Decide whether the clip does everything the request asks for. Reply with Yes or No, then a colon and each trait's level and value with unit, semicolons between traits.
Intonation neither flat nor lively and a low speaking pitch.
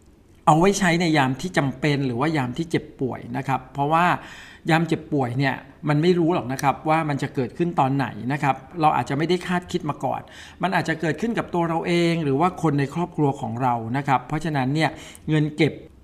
No: average, 3.6 semitones; medium, 150 Hz